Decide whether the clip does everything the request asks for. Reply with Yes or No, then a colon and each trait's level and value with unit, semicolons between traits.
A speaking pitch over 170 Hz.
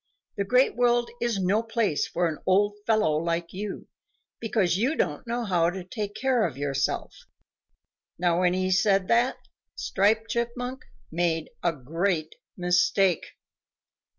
Yes: high, 190 Hz